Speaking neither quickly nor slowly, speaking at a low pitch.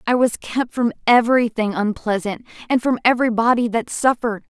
No: average, 145 wpm; high, 230 Hz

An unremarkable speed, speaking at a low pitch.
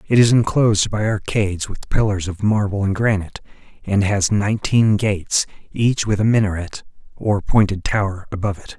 Yes: average, 165 wpm; low, 100 Hz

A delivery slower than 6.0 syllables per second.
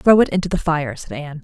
No: 6.5 syllables/s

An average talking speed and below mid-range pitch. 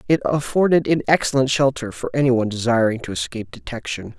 Yes: average, 160 wpm; low, 125 Hz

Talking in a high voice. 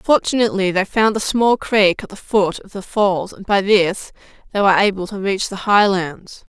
Yes: high, 200 Hz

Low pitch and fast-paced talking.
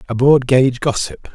No: low, 130 Hz; average, 180 wpm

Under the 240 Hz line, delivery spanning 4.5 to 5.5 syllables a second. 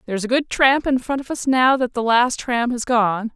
No: high, 245 Hz; 5.0 syllables/s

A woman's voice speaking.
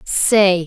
Yes: female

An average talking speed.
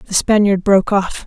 Yes: average, 190 wpm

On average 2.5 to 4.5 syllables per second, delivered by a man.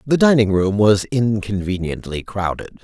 Yes: 4.4 syllables/s; male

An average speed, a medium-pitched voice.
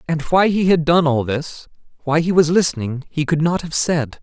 No: fast, 225 wpm; medium, 155 Hz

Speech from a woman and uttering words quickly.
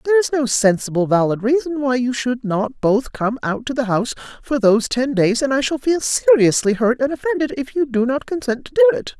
Yes: female; fast, 235 wpm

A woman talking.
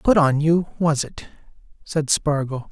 No: male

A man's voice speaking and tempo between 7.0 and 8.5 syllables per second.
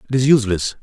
Yes: male; 8.1 syllables/s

